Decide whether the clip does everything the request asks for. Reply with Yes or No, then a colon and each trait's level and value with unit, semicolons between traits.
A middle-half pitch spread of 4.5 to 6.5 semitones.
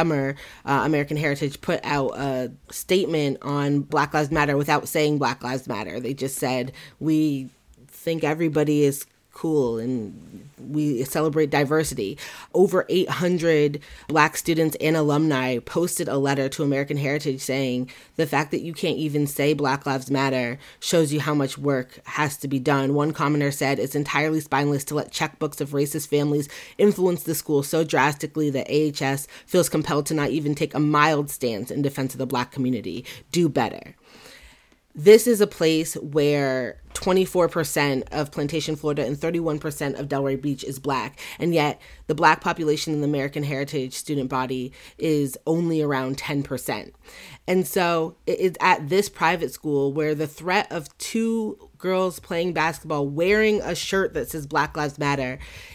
No: narrow, 2.4 semitones